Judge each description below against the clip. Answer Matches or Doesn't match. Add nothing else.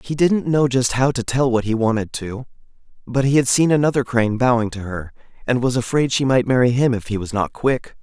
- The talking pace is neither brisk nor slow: Doesn't match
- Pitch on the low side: Matches